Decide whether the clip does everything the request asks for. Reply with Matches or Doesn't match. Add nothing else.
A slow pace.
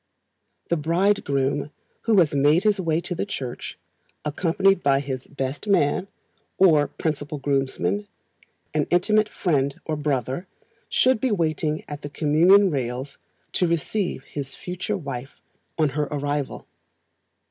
Matches